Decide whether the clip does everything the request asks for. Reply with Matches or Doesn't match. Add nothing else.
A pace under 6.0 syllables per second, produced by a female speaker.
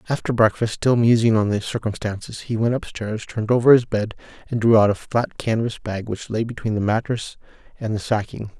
Doesn't match